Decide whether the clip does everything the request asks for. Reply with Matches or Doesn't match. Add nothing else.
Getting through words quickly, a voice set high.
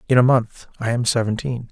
Doesn't match